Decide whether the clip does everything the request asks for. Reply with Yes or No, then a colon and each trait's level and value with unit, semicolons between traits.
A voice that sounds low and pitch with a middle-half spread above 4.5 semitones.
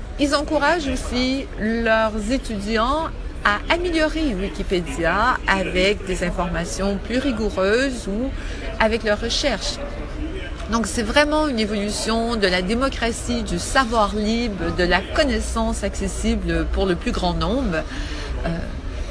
No: high, 220 Hz; average, 5.1 semitones